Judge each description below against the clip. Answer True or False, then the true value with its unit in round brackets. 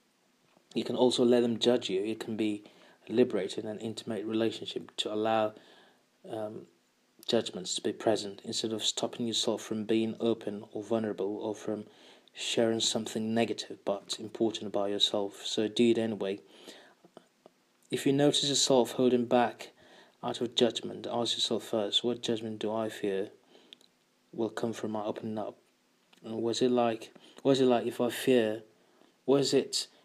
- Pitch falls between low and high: False (115 Hz)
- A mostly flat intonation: True (1.9 semitones)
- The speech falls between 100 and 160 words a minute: True (155 wpm)